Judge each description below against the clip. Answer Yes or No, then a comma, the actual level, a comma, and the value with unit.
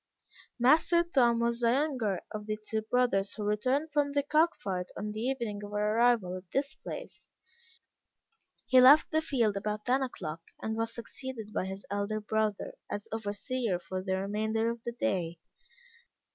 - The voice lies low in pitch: No, high, 220 Hz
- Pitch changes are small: No, average, 3.8 semitones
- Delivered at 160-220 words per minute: Yes, average, 170 wpm